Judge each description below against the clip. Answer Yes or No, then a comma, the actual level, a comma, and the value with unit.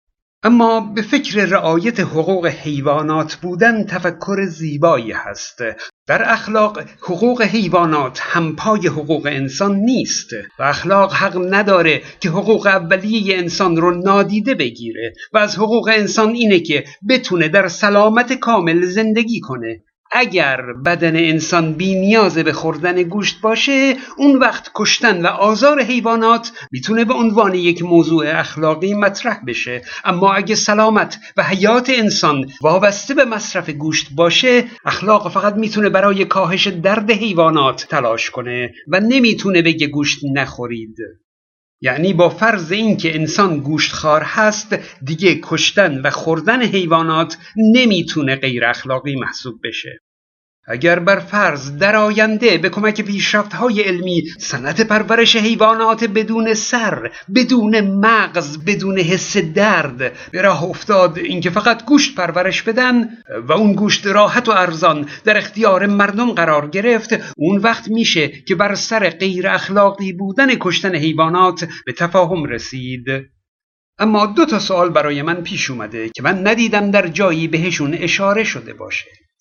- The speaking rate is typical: Yes, average, 135 wpm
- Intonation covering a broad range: No, average, 5.0 semitones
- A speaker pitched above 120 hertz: Yes, high, 190 Hz